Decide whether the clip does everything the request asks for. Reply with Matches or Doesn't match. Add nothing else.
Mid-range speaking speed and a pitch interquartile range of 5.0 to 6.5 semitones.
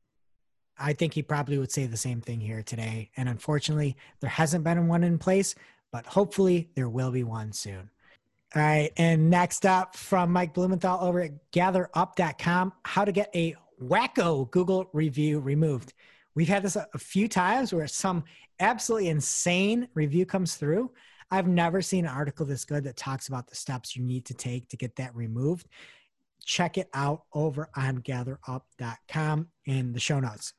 Matches